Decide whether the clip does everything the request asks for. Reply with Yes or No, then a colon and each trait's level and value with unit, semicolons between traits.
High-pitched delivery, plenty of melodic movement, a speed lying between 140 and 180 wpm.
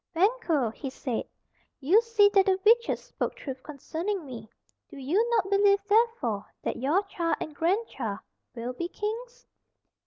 Yes: very high, 370 Hz; wide, 7.9 semitones; average, 150 wpm